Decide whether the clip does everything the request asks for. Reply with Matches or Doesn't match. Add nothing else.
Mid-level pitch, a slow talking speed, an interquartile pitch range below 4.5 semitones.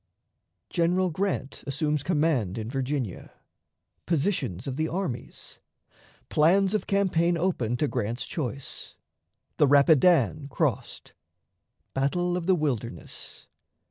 Doesn't match